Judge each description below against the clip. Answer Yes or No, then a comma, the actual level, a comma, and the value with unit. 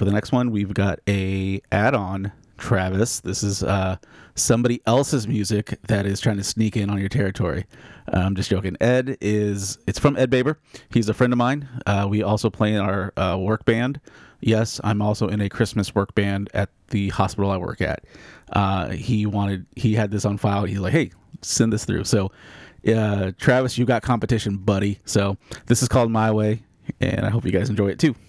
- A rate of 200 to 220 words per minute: Yes, fast, 205 wpm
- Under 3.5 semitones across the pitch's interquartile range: Yes, average, 3.0 semitones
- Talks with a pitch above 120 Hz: No, low, 105 Hz